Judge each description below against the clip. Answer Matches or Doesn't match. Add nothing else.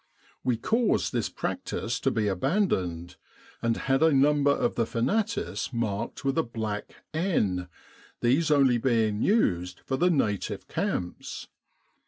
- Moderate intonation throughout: Doesn't match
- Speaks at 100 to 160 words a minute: Matches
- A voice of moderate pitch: Doesn't match